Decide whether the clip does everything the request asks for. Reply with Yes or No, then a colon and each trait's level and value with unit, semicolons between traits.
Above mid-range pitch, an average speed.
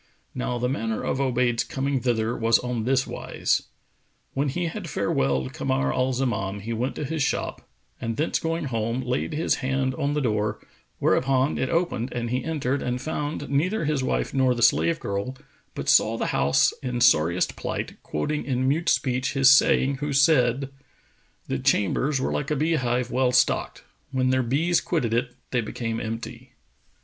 No: low, 130 Hz; average, 180 wpm